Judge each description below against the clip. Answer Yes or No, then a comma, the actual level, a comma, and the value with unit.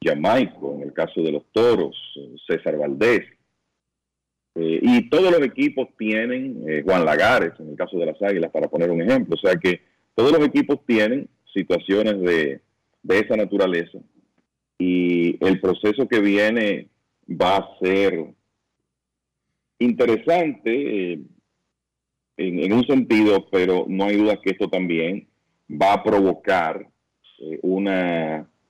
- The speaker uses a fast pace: No, average, 140 wpm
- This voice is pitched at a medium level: No, very low, 95 Hz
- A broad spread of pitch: Yes, wide, 6.5 semitones